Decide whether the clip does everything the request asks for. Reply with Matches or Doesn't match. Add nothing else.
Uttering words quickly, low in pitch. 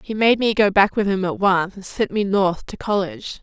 Doesn't match